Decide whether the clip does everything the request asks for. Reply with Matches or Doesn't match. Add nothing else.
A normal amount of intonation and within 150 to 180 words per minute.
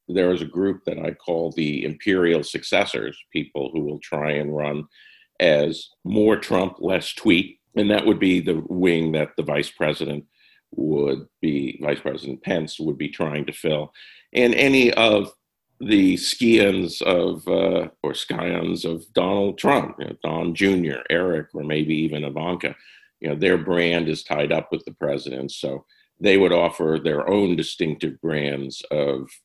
Matches